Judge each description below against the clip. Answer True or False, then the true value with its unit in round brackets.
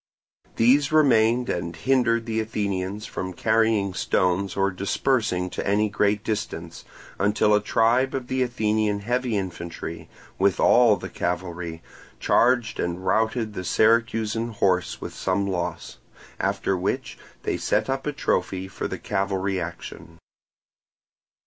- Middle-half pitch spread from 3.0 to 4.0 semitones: True (3.7 semitones)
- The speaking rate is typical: False (130 wpm)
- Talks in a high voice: False (105 Hz)